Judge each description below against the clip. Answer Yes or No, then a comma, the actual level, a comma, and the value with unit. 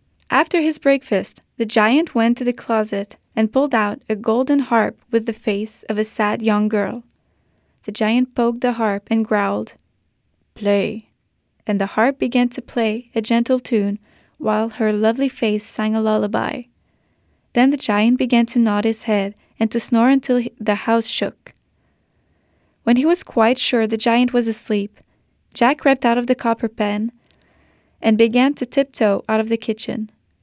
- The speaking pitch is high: Yes, high, 225 Hz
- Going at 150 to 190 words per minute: Yes, average, 170 wpm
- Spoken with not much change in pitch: Yes, narrow, 2.3 semitones